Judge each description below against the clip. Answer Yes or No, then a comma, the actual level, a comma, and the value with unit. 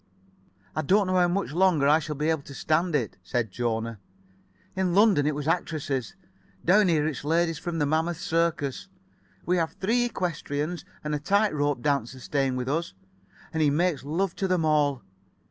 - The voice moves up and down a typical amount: Yes, average, 3.7 semitones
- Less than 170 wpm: No, average, 180 wpm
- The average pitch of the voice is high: No, medium, 155 Hz